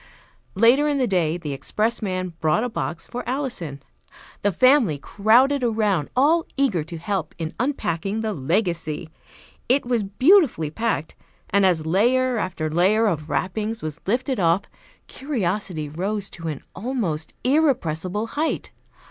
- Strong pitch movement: Yes, wide, 6.9 semitones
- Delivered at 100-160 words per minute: Yes, average, 140 wpm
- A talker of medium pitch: No, high, 200 Hz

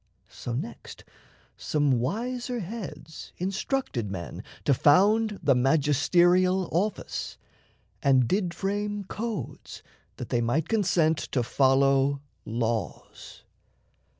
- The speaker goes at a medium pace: No, slow, 95 wpm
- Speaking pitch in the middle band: Yes, medium, 160 Hz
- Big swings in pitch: Yes, wide, 7.2 semitones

